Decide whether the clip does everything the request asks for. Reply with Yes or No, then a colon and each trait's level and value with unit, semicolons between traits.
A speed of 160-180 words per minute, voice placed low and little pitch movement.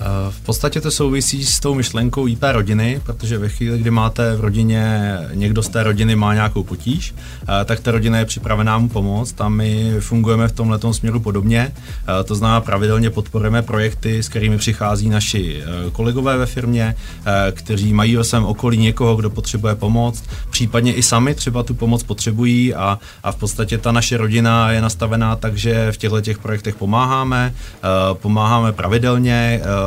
Yes: average, 165 wpm; low, 110 Hz; narrow, 1.8 semitones